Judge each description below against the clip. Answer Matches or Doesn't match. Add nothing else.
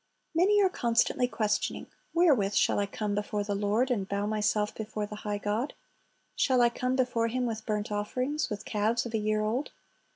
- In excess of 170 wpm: Matches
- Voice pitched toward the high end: Matches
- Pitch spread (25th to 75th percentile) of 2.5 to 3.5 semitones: Matches